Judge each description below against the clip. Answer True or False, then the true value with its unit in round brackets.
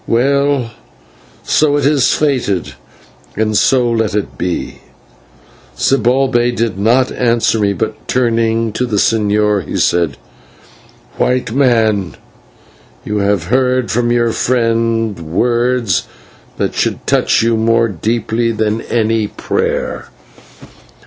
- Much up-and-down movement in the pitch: False (2.9 semitones)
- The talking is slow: True (115 wpm)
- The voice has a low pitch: True (115 Hz)